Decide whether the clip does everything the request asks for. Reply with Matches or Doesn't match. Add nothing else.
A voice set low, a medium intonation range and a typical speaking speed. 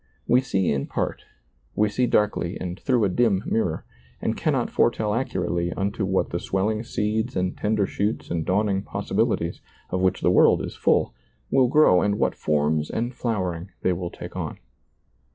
Matches